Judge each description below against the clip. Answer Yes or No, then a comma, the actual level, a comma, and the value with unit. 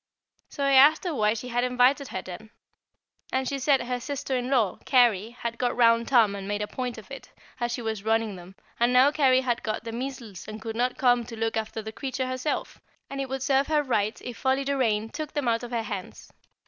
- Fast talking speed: Yes, fast, 235 wpm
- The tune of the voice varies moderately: Yes, average, 3.1 semitones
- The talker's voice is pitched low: No, high, 245 Hz